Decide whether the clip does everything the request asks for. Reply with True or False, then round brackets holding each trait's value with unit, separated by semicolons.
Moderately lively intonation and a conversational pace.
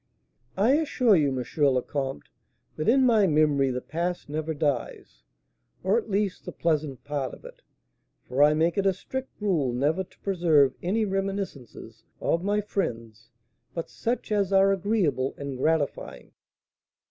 False (5.9 semitones; 155 wpm)